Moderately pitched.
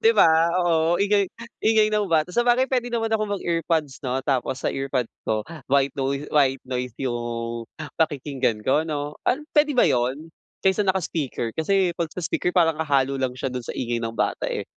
Yes: medium, 150 Hz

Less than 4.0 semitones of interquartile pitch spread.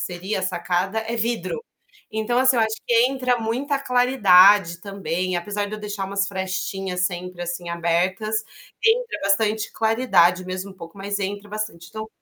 Yes: average, 3.3 semitones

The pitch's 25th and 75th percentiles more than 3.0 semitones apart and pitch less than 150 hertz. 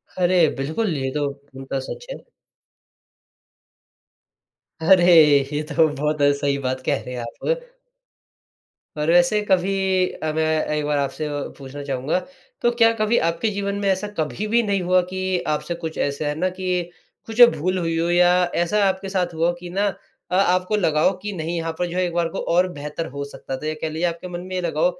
No: average, 3.8 semitones; medium, 175 Hz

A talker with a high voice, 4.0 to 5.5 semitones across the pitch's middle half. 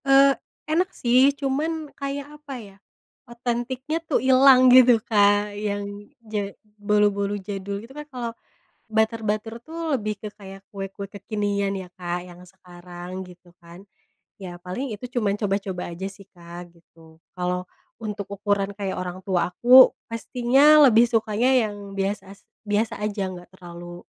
Yes: high, 205 Hz; average, 4.4 semitones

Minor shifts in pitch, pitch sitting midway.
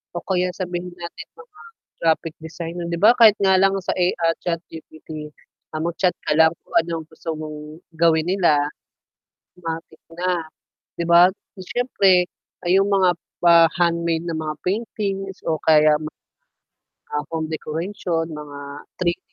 Yes: narrow, 2.3 semitones; medium, 170 Hz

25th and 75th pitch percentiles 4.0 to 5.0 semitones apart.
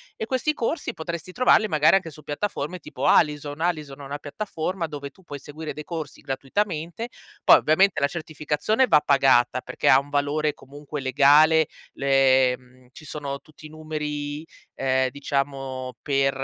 No: narrow, 2.6 semitones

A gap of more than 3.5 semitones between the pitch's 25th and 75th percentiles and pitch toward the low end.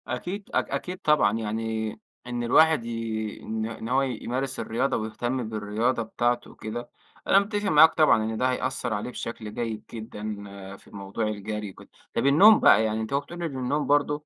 Yes: average, 4.2 semitones; low, 120 Hz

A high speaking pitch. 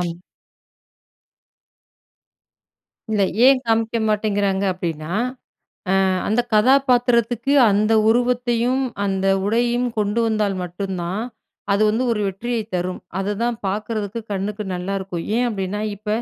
Yes: high, 210 Hz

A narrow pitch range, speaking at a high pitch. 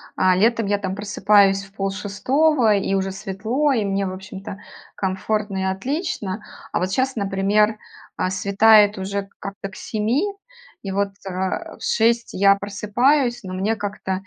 Yes: narrow, 2.2 semitones; high, 200 Hz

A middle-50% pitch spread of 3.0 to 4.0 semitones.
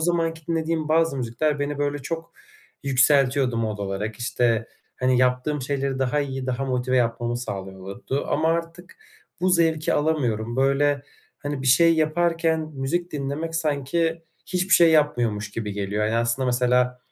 No: average, 4.6 semitones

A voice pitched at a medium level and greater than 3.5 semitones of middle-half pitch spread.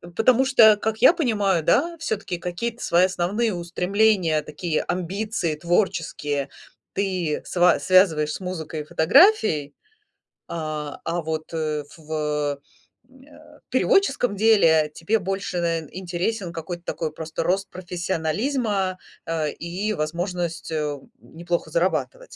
Yes: medium, 175 Hz; average, 4.6 semitones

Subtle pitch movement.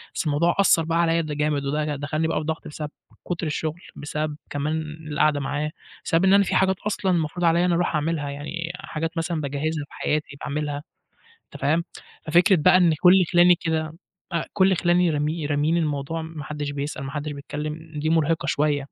Yes: narrow, 2.3 semitones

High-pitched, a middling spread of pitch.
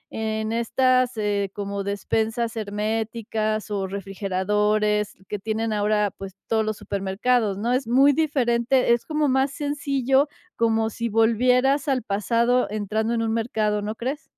Yes: high, 220 Hz; average, 3.1 semitones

